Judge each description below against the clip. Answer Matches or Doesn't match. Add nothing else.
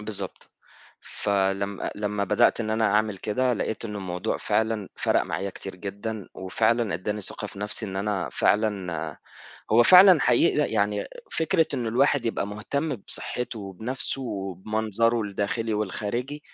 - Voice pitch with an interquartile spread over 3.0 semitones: Doesn't match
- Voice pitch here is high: Doesn't match